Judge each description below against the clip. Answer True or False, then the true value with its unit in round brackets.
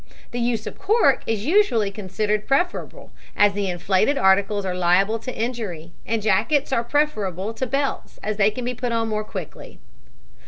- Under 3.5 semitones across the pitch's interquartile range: False (3.9 semitones)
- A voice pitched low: False (215 Hz)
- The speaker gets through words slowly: False (170 wpm)